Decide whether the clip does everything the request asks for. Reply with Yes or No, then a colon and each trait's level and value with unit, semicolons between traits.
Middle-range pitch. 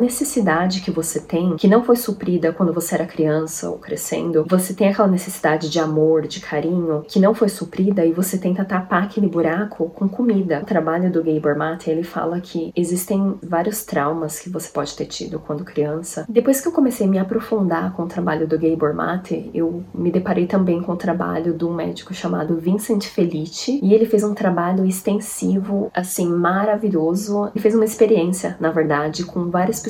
Yes: medium, 175 Hz